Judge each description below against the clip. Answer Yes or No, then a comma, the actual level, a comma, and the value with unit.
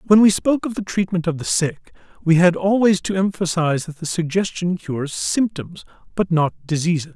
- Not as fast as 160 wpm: No, average, 185 wpm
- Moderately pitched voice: Yes, medium, 175 Hz